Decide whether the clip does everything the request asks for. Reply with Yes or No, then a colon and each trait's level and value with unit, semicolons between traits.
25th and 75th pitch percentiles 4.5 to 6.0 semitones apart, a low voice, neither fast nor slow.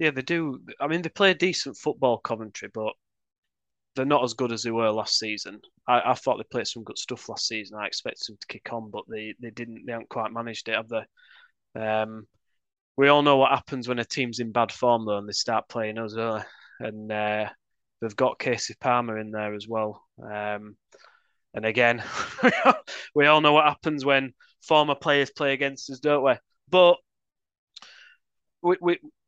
Yes: average, 5.0 semitones; low, 120 Hz; average, 195 wpm